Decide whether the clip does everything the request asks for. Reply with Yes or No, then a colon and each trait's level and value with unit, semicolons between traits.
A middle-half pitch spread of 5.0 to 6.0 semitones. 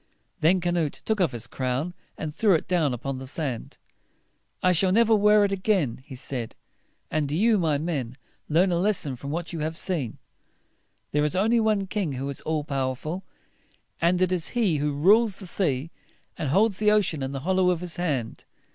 Yes: average, 5.3 semitones